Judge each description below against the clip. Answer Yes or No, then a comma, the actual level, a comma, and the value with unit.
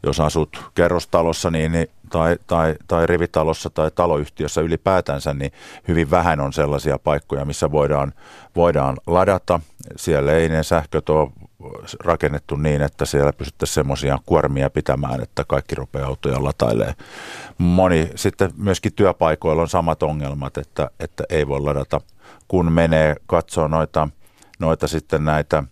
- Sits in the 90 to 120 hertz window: No, very low, 80 Hz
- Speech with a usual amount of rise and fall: Yes, average, 3.0 semitones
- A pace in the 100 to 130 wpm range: No, average, 140 wpm